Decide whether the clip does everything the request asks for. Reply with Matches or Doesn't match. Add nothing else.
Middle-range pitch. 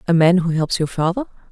Matches